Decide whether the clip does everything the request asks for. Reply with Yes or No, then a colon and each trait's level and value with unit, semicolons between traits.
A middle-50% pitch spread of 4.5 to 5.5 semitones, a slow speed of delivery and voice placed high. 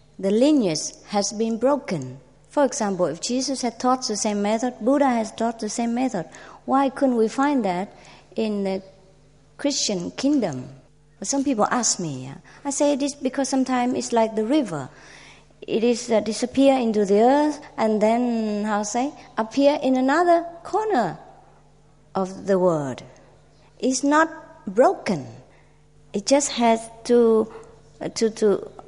No: average, 5.1 semitones; average, 150 wpm; high, 230 Hz